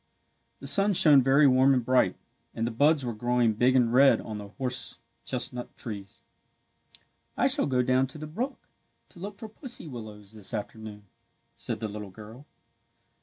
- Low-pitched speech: Yes, low, 125 Hz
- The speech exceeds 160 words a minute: Yes, average, 170 wpm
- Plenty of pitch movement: No, average, 4.3 semitones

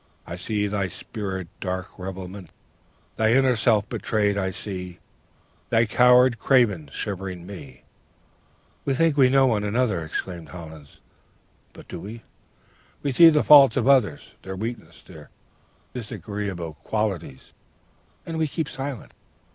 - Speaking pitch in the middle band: No, low, 105 Hz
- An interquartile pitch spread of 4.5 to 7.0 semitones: Yes, average, 5.3 semitones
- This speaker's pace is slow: Yes, slow, 130 wpm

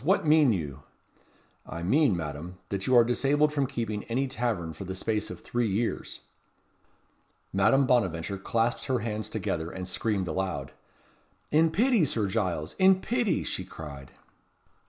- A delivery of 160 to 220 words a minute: No, average, 150 wpm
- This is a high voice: No, low, 110 Hz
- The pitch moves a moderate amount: No, wide, 6.9 semitones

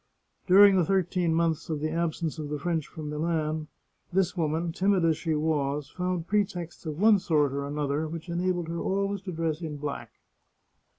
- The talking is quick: No, average, 180 wpm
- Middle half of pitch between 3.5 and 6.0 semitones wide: No, average, 2.9 semitones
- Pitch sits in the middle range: Yes, medium, 165 Hz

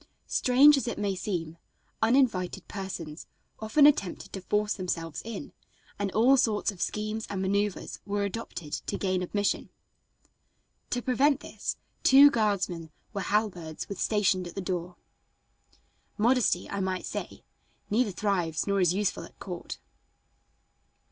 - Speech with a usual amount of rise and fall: Yes, average, 3.4 semitones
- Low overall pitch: No, high, 200 Hz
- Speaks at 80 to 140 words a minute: Yes, slow, 135 wpm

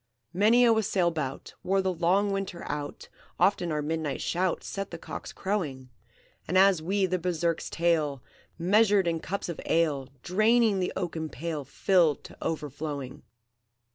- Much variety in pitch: No, average, 3.9 semitones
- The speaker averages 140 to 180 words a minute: Yes, average, 145 wpm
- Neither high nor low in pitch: Yes, medium, 170 Hz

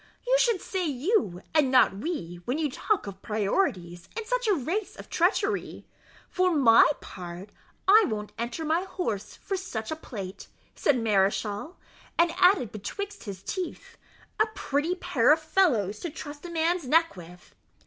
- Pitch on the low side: No, very high, 295 Hz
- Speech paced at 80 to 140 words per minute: No, average, 160 wpm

